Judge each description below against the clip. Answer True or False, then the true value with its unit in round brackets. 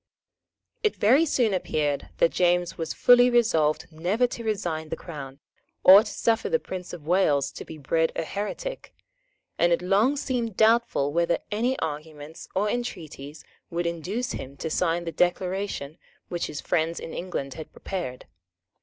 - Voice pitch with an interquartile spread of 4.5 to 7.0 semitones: True (5.5 semitones)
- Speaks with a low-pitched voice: False (175 Hz)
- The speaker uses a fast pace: False (160 wpm)